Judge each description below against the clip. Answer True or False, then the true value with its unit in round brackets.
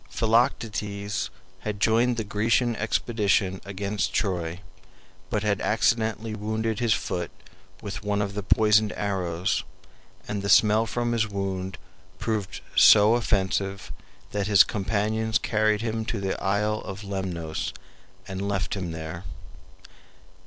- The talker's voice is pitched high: False (105 Hz)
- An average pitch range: False (2.2 semitones)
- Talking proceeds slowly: True (125 wpm)